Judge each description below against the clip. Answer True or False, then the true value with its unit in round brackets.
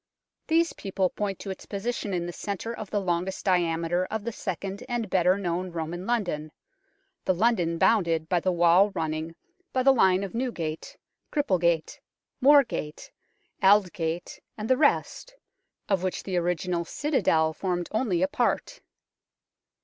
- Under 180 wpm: True (145 wpm)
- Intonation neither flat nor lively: True (4.0 semitones)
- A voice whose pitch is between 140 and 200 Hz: True (185 Hz)